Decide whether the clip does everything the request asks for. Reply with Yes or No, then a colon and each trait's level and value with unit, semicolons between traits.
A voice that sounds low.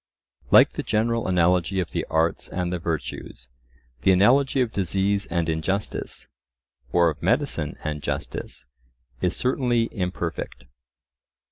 Yes: very low, 90 Hz